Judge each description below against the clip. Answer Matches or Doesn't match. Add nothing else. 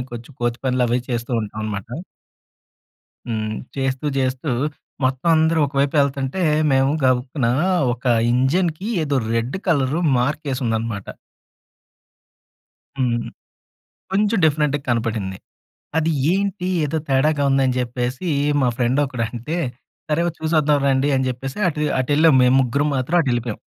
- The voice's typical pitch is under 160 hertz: Matches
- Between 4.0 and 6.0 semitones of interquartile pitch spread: Doesn't match